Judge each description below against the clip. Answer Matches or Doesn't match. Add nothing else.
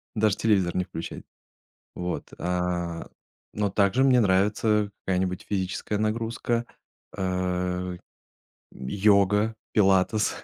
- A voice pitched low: Matches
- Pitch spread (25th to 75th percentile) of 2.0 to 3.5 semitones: Matches